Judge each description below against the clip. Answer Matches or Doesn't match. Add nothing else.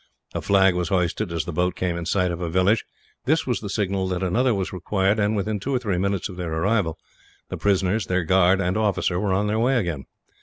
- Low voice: Matches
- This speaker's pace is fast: Matches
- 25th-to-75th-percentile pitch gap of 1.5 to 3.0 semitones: Matches